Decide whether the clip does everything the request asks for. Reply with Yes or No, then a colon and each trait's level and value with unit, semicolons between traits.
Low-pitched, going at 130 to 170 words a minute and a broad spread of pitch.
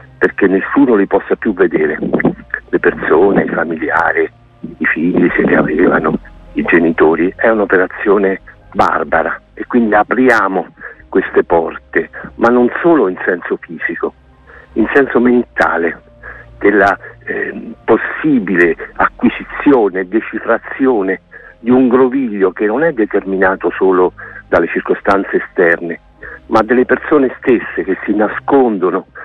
No: low, 120 Hz; slow, 115 wpm; wide, 6.8 semitones